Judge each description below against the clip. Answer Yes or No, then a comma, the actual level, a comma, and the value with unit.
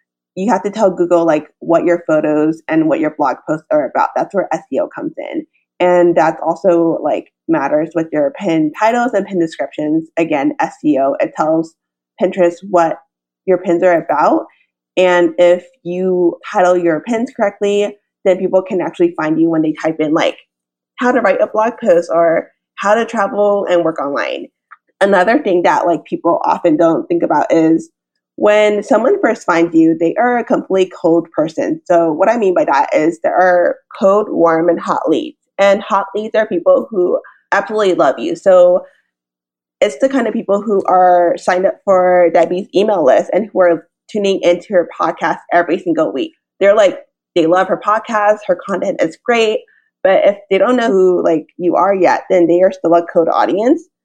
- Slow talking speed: No, average, 190 wpm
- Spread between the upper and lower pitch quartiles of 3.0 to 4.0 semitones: No, average, 4.7 semitones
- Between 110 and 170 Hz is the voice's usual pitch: No, medium, 180 Hz